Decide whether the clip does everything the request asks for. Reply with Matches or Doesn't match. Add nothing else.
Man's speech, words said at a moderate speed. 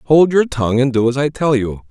Doesn't match